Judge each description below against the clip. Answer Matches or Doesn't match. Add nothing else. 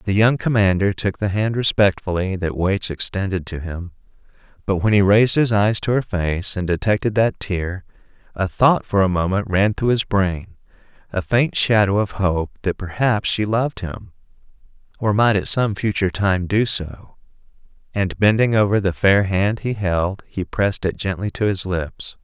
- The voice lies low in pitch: Matches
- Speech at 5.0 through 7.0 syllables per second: Doesn't match